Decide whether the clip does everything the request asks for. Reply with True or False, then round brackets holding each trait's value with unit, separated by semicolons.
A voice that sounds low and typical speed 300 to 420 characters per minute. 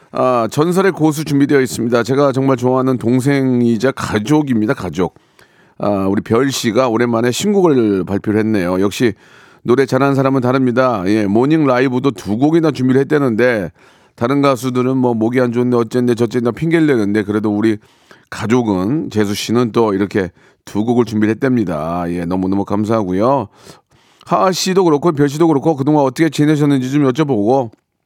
True (125 Hz; 370 characters per minute)